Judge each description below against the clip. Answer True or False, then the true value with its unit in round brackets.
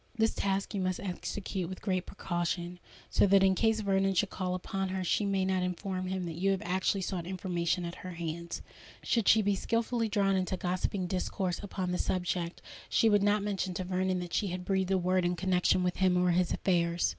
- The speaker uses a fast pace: True (215 wpm)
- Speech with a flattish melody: True (1.5 semitones)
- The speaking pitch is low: False (185 Hz)